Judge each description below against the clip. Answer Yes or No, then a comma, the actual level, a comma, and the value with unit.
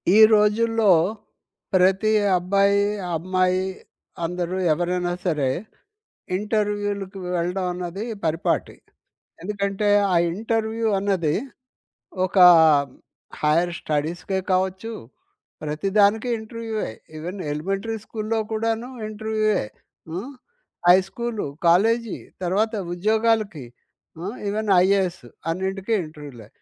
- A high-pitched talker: Yes, high, 195 Hz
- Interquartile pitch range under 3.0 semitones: No, average, 3.5 semitones